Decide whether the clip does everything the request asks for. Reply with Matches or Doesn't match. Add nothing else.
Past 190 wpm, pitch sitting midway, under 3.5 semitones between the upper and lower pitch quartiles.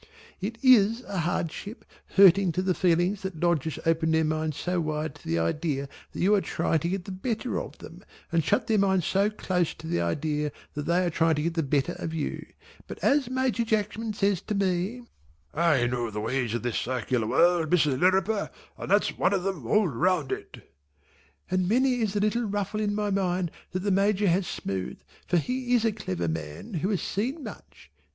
Doesn't match